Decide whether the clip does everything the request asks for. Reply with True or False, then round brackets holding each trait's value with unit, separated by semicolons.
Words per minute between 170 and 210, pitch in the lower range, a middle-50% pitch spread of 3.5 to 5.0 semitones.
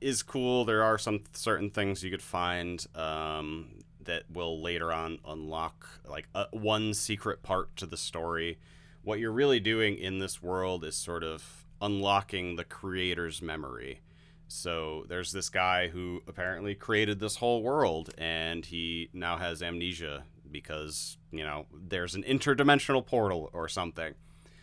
False (150 wpm; 90 Hz; 3.8 semitones)